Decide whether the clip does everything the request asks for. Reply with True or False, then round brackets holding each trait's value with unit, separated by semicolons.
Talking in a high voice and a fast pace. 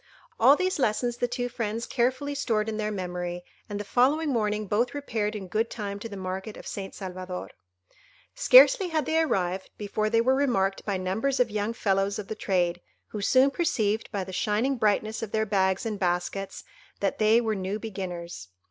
False (215 Hz; 190 wpm)